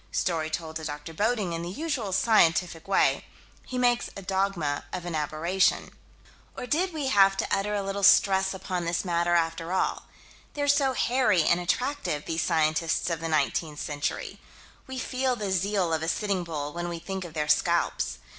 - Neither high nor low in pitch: Yes, medium, 180 Hz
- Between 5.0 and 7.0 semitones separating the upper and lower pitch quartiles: No, average, 4.1 semitones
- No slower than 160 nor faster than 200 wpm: Yes, average, 185 wpm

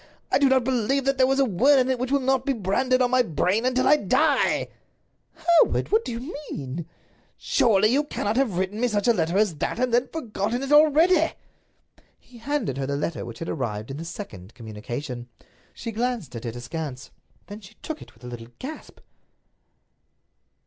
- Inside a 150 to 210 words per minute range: Yes, average, 200 wpm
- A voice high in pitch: Yes, high, 225 Hz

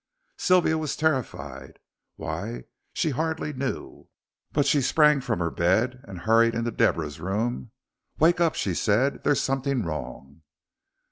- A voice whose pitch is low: Yes, low, 120 Hz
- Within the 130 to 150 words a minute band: Yes, slow, 135 wpm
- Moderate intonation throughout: No, wide, 8.9 semitones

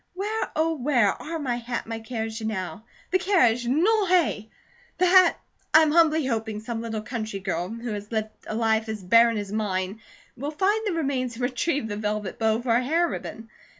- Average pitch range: No, wide, 6.3 semitones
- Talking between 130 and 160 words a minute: No, average, 200 wpm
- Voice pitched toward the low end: No, high, 235 Hz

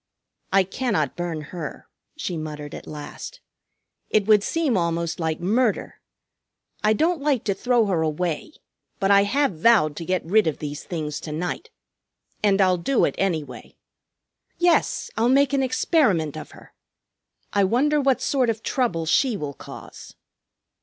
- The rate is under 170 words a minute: Yes, average, 155 wpm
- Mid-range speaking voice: No, high, 195 Hz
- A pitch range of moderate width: No, wide, 7.6 semitones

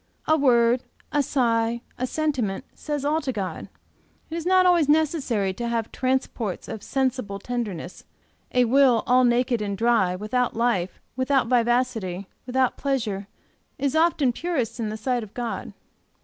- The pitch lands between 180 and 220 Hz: No, high, 245 Hz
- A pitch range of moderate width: Yes, average, 3.5 semitones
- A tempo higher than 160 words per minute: No, average, 150 wpm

